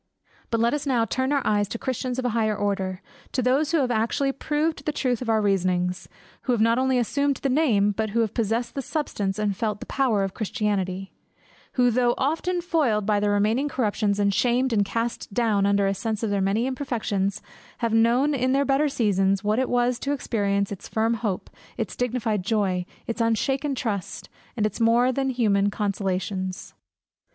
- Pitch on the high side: Yes, high, 225 Hz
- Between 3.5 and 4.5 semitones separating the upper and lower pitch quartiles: Yes, average, 4.1 semitones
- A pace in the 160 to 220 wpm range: Yes, average, 195 wpm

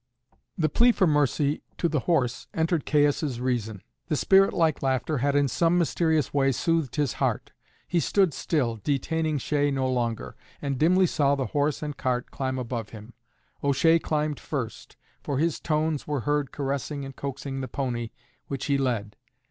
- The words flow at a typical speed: Yes, average, 170 wpm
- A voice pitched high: No, medium, 140 Hz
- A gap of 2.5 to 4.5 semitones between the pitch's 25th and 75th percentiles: Yes, average, 3.2 semitones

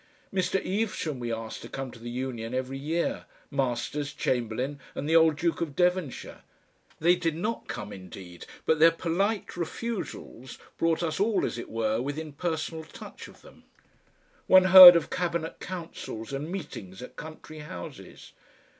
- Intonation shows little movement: No, wide, 5.6 semitones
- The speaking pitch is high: No, medium, 155 Hz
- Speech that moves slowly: No, average, 155 wpm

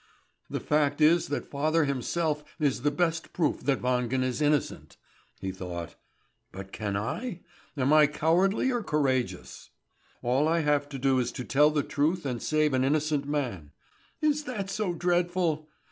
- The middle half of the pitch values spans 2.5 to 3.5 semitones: No, average, 4.1 semitones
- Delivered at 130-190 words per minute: Yes, average, 160 wpm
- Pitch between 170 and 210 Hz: No, medium, 150 Hz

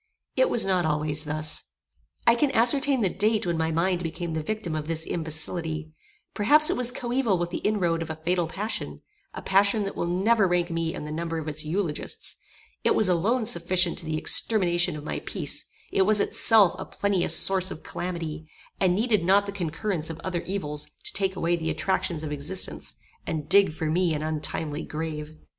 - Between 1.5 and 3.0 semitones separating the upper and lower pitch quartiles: No, average, 4.0 semitones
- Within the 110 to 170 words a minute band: No, average, 195 wpm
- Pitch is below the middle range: No, medium, 175 Hz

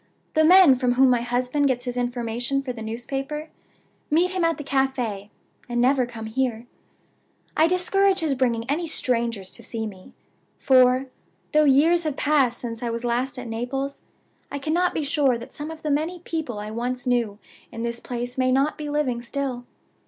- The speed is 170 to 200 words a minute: Yes, average, 185 wpm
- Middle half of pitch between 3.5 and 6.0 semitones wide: Yes, average, 3.8 semitones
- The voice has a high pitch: Yes, very high, 255 Hz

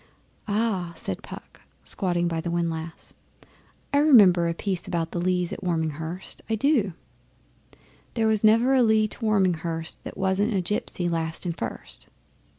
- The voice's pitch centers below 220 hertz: Yes, medium, 185 Hz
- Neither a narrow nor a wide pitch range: Yes, average, 4.2 semitones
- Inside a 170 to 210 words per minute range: No, average, 155 wpm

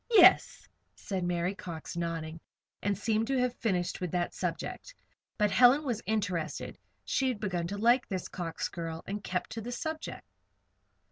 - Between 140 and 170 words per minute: Yes, average, 160 wpm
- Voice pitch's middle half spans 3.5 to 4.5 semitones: No, average, 5.3 semitones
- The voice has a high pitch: Yes, high, 200 Hz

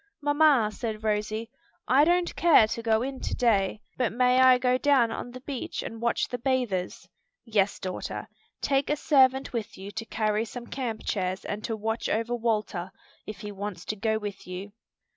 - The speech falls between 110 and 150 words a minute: No, average, 185 wpm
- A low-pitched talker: No, high, 225 Hz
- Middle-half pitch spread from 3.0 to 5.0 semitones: Yes, average, 3.5 semitones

